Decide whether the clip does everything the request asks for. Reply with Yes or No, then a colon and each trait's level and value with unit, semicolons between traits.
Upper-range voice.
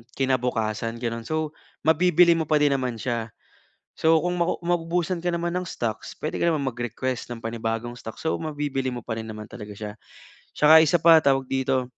No: low, 135 Hz